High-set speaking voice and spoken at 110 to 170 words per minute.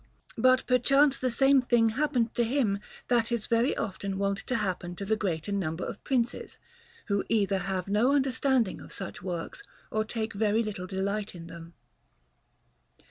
Yes: high, 215 Hz; average, 165 wpm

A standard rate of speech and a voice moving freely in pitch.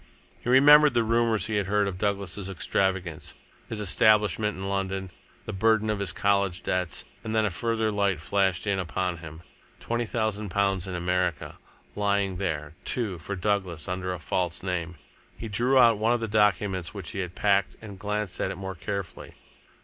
No: average, 180 wpm; average, 2.8 semitones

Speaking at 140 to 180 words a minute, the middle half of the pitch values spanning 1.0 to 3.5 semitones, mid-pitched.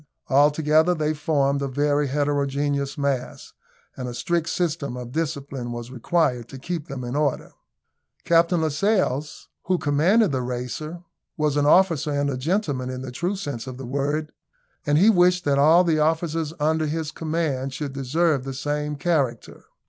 Yes: average, 165 wpm; average, 3.1 semitones; medium, 145 Hz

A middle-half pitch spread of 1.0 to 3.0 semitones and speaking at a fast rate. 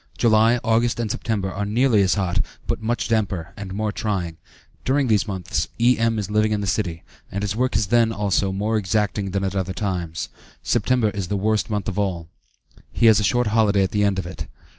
Yes: narrow, 2.6 semitones; fast, 210 wpm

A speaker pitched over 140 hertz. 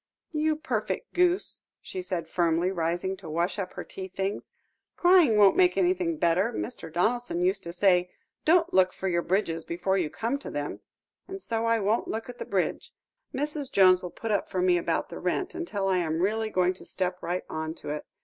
Yes: high, 190 Hz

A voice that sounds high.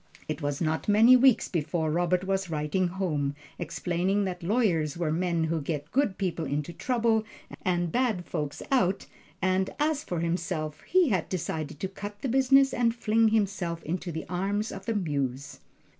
No: medium, 180 Hz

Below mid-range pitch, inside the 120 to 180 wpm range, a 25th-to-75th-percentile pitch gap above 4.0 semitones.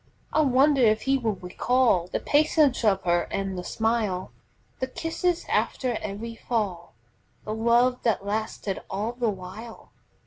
No: high, 225 Hz; average, 145 wpm; average, 4.4 semitones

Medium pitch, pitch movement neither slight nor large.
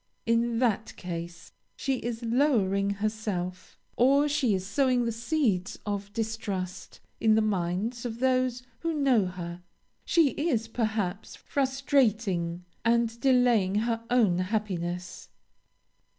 No: high, 225 Hz; average, 4.6 semitones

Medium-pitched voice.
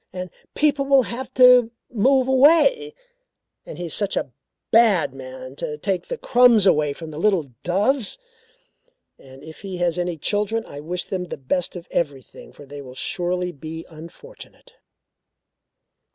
Yes: medium, 180 Hz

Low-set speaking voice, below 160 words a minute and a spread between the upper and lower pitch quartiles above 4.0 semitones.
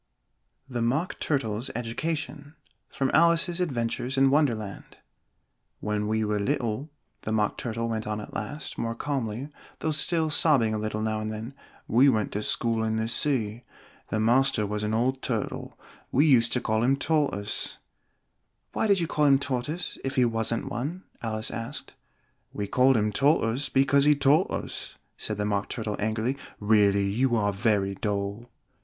No: low, 115 Hz; average, 165 wpm; average, 4.4 semitones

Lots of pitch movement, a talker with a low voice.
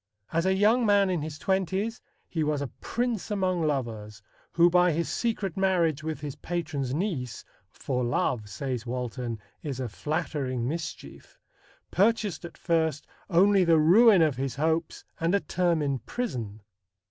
No: wide, 5.9 semitones; medium, 160 Hz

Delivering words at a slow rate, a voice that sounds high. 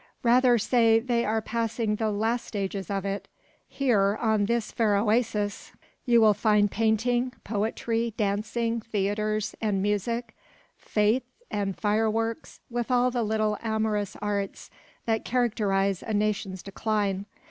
Yes: slow, 130 wpm; high, 215 Hz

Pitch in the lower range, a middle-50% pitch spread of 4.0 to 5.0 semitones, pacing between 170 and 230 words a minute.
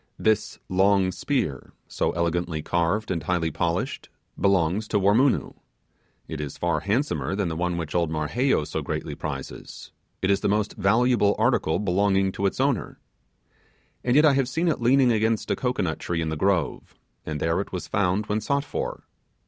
Yes: very low, 95 Hz; average, 4.7 semitones; average, 175 wpm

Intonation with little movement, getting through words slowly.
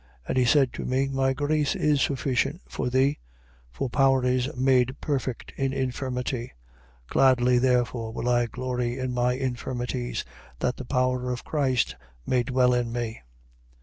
No: narrow, 1.5 semitones; average, 150 wpm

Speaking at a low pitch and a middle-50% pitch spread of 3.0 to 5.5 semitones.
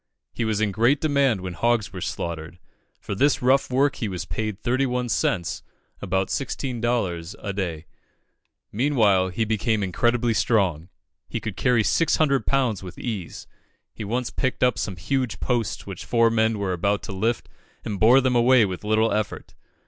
Yes: low, 110 Hz; average, 4.4 semitones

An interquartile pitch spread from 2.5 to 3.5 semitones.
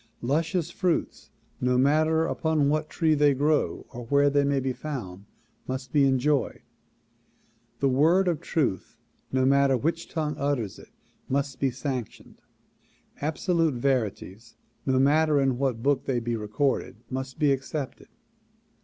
Yes: average, 2.9 semitones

